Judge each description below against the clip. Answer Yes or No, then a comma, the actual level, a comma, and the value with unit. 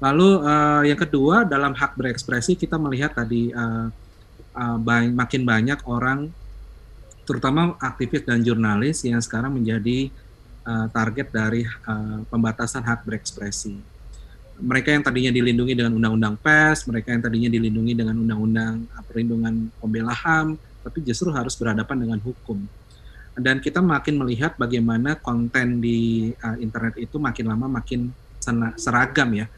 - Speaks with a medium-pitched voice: No, low, 120 Hz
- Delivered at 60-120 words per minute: No, fast, 140 wpm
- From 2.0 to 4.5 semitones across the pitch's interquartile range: Yes, average, 2.8 semitones